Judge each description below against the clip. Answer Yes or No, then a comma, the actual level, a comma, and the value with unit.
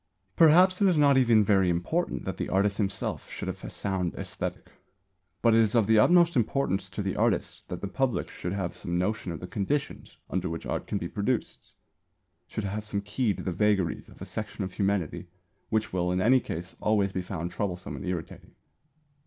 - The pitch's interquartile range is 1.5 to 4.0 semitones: Yes, average, 3.7 semitones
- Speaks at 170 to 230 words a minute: Yes, average, 200 wpm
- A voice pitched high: No, low, 100 Hz